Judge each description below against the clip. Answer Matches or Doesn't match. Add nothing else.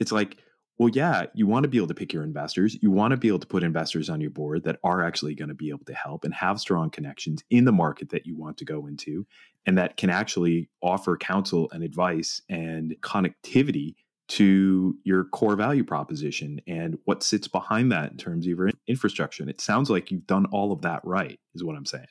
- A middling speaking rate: Doesn't match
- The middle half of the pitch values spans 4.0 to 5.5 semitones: Matches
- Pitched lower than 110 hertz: Matches